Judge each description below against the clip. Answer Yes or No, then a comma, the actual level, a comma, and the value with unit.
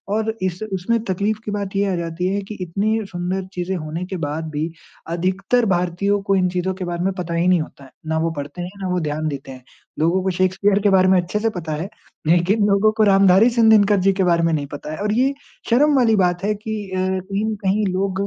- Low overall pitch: No, medium, 185 Hz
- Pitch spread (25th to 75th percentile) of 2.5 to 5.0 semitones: Yes, average, 2.9 semitones